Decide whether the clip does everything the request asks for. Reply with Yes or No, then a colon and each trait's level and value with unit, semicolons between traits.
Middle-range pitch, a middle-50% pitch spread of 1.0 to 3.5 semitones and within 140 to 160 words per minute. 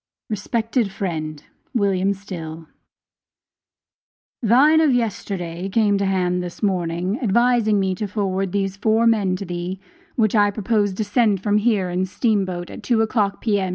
No: high, 200 Hz; average, 3.0 semitones; average, 155 wpm